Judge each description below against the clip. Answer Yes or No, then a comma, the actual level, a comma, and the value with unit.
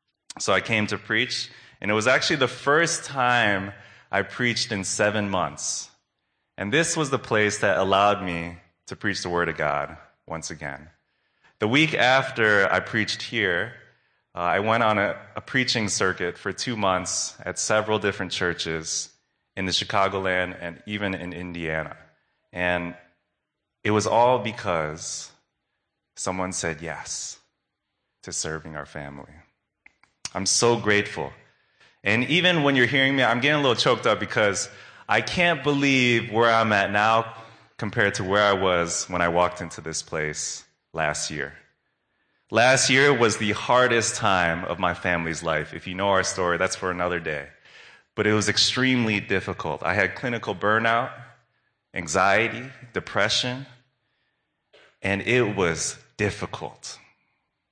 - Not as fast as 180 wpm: Yes, average, 150 wpm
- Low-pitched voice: Yes, low, 100 Hz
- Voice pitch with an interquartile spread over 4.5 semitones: Yes, average, 5.1 semitones